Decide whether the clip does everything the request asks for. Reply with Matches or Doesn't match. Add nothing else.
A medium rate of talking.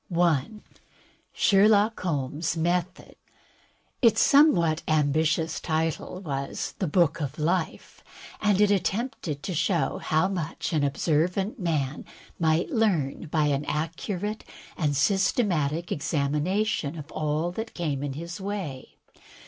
Doesn't match